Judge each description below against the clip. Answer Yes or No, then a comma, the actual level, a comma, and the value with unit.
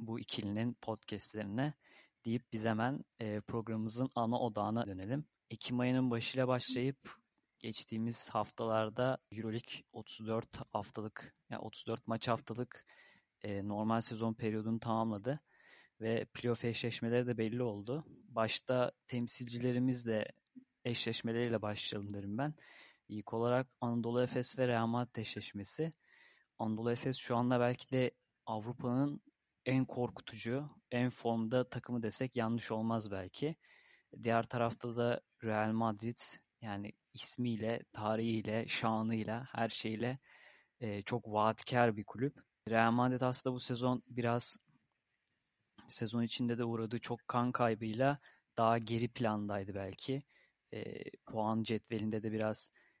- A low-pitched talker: Yes, low, 115 Hz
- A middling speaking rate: Yes, average, 110 wpm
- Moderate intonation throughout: No, narrow, 2.0 semitones